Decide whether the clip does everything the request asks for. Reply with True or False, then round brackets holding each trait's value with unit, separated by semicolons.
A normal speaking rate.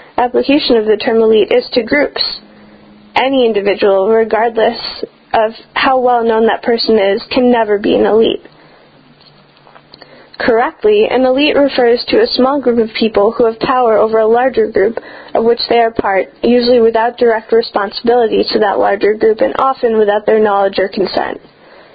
True (165 wpm)